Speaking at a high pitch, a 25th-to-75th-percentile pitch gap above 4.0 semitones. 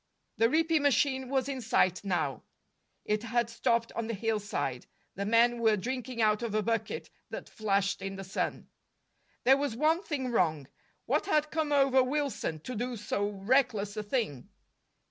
Yes: high, 230 Hz; average, 4.5 semitones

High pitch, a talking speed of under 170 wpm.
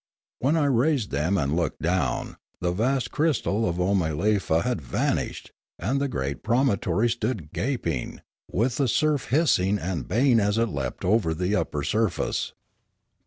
No: low, 105 Hz; average, 155 wpm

